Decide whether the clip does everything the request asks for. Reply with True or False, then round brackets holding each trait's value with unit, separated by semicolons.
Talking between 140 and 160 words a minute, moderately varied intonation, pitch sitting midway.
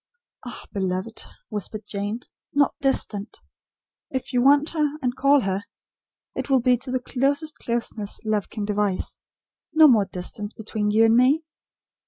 False (150 wpm; 4.6 semitones; 230 Hz)